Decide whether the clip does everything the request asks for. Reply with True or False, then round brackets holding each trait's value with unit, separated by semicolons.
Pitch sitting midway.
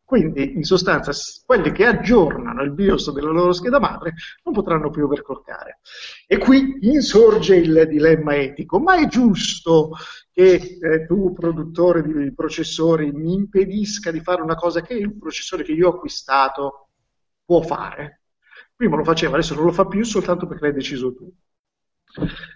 True (170 Hz)